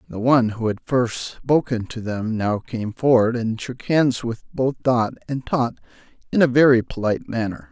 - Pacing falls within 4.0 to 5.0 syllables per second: Yes, 4.7 syllables/s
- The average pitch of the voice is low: Yes, low, 120 Hz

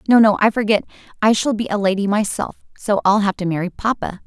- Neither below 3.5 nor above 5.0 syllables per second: No, 6.1 syllables/s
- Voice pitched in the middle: No, high, 205 Hz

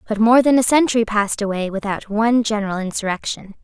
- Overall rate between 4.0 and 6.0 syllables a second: No, 6.5 syllables/s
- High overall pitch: Yes, high, 215 Hz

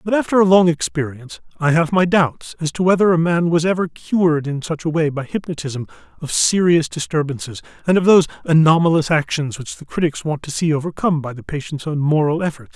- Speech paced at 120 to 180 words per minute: No, fast, 205 wpm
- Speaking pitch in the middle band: Yes, medium, 160 Hz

